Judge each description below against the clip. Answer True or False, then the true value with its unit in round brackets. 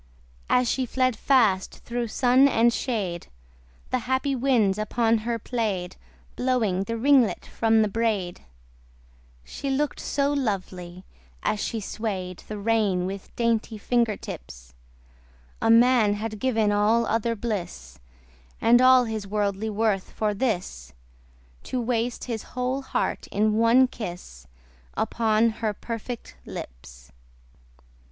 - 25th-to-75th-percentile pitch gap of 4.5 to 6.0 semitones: False (3.3 semitones)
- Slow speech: True (125 wpm)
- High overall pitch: True (225 Hz)